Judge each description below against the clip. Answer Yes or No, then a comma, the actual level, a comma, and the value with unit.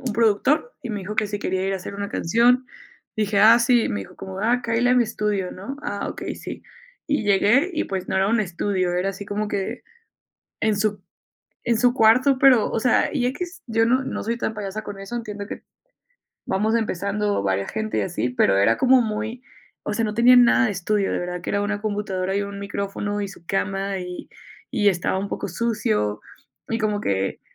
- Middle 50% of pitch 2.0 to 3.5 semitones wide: Yes, average, 3.2 semitones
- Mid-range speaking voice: No, high, 210 Hz